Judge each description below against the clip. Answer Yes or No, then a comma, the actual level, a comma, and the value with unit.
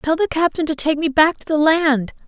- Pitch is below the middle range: No, very high, 310 Hz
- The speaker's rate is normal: No, fast, 265 wpm